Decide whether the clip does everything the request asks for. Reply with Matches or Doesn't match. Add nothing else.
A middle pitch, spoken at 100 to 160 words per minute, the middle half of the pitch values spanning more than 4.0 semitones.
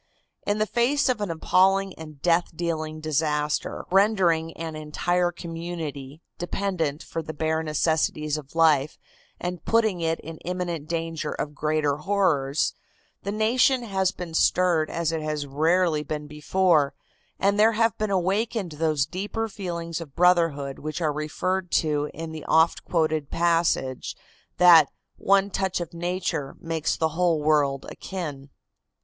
Doesn't match